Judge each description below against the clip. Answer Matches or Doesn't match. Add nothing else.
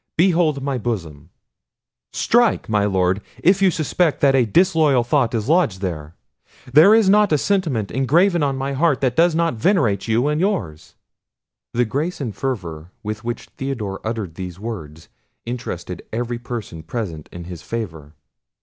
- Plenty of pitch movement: Matches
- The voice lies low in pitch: Matches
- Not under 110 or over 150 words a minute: Doesn't match